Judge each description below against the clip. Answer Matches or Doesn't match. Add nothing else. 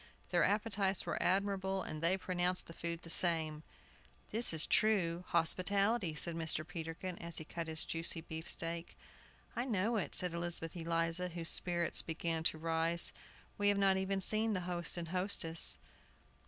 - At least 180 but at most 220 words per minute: Doesn't match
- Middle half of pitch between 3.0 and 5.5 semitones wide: Doesn't match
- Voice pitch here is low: Doesn't match